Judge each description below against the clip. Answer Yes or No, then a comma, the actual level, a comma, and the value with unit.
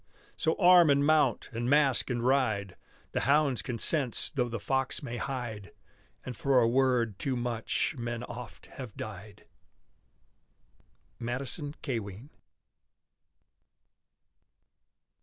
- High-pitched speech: No, low, 125 Hz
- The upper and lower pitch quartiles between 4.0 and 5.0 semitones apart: No, average, 3.1 semitones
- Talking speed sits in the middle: No, slow, 115 wpm